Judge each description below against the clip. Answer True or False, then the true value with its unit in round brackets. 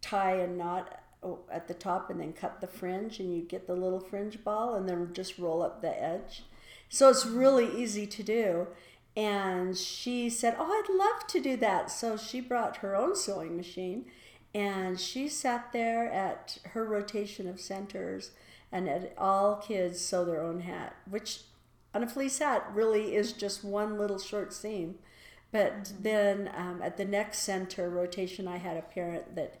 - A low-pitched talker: False (200 Hz)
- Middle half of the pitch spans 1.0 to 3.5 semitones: True (3.2 semitones)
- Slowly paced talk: False (180 wpm)